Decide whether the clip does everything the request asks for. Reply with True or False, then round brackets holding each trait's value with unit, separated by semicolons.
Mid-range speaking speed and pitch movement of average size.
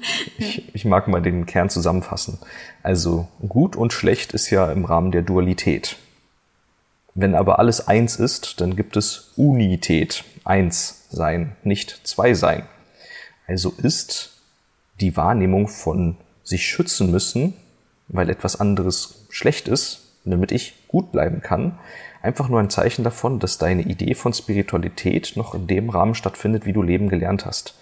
True (150 wpm; 3.5 semitones)